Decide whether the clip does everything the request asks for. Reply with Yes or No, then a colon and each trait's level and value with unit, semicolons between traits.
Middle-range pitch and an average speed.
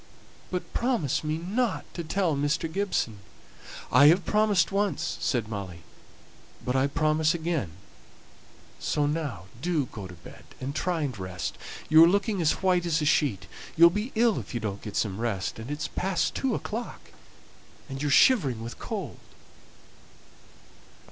Yes: medium, 155 Hz; average, 155 wpm